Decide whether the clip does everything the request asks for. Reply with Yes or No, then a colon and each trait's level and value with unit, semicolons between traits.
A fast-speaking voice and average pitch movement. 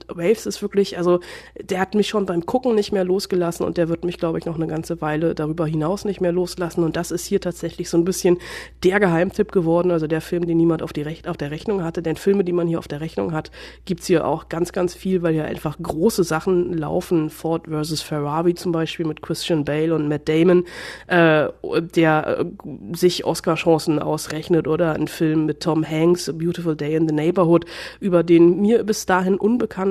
No: fast, 215 wpm; narrow, 2.3 semitones